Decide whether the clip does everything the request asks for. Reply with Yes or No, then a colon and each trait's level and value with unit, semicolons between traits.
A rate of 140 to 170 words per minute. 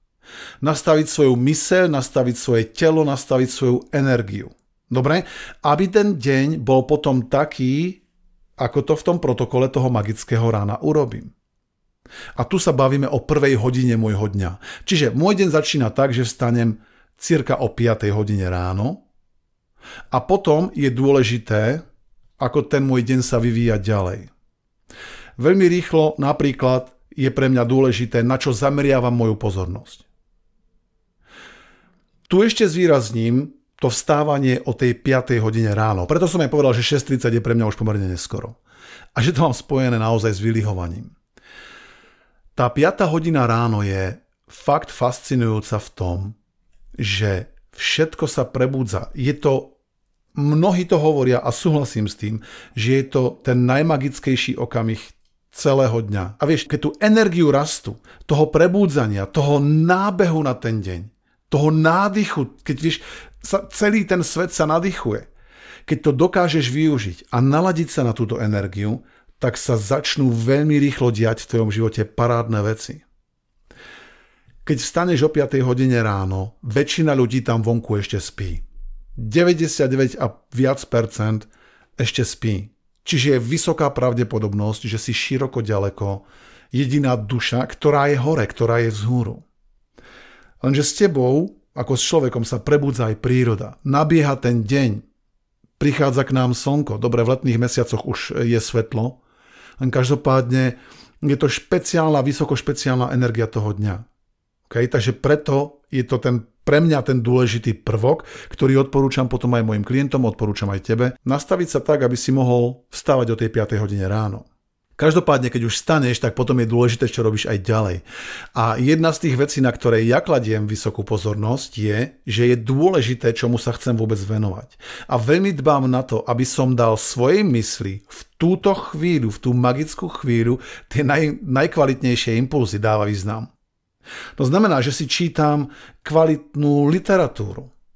Yes: average, 145 wpm